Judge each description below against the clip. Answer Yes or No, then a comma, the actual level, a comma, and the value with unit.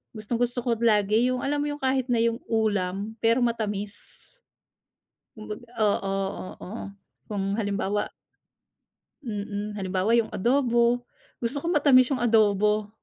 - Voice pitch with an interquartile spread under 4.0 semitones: Yes, average, 2.9 semitones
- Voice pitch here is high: Yes, high, 220 Hz